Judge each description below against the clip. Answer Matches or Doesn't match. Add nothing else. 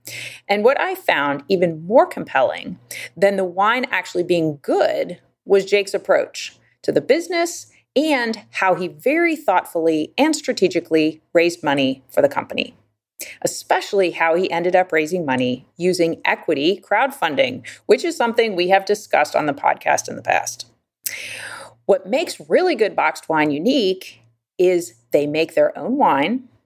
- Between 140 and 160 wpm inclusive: Matches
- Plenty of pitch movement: Matches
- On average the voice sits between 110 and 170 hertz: Doesn't match